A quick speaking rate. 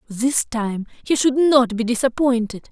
No: average, 155 wpm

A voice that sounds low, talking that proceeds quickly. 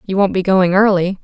No: high, 190 Hz; fast, 245 wpm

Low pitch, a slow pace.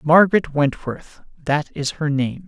No: medium, 150 Hz; slow, 120 wpm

